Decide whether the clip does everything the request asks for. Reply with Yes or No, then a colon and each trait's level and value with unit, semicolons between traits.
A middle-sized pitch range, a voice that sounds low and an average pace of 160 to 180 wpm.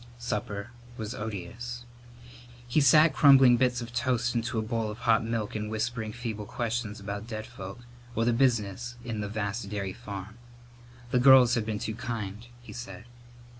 No: narrow, 2.3 semitones; low, 115 Hz; average, 170 wpm